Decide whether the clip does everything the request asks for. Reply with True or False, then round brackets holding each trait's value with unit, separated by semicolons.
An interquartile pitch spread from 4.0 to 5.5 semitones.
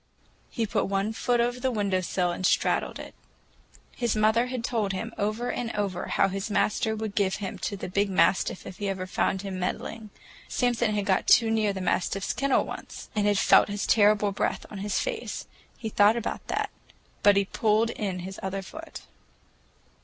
False (2.5 semitones)